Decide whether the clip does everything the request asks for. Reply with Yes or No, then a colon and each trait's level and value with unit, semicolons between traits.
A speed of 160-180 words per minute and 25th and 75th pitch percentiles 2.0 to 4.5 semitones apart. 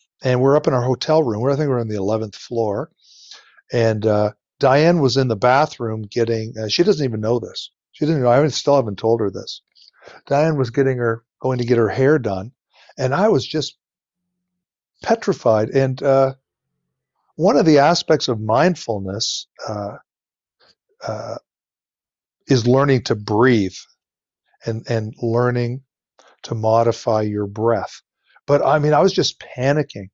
Yes: average, 165 wpm; average, 4.1 semitones